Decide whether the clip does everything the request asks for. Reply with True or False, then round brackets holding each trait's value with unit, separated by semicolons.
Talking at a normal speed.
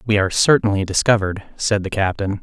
True (175 wpm)